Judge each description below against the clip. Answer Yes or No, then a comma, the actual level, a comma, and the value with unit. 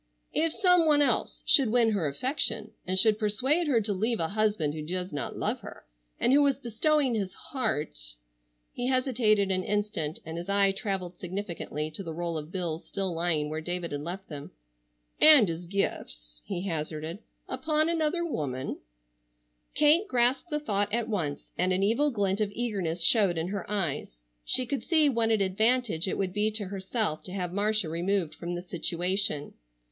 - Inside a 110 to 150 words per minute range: No, average, 175 wpm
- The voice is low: No, high, 195 Hz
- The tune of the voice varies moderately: No, wide, 6.2 semitones